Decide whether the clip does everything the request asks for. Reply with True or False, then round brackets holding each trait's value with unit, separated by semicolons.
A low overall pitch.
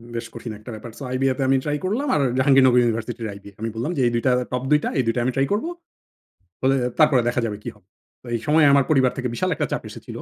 True (130 Hz)